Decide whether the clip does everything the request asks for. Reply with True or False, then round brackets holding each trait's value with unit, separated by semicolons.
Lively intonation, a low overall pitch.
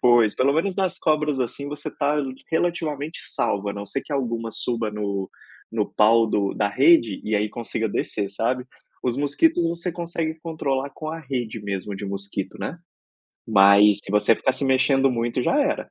True (6.3 semitones; 125 Hz)